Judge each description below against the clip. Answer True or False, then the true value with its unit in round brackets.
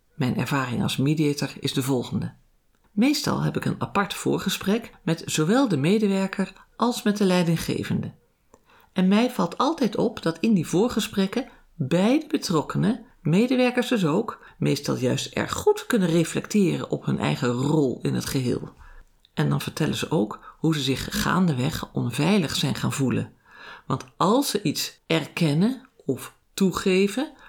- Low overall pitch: False (190 Hz)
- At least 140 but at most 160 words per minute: True (150 wpm)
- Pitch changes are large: True (7.2 semitones)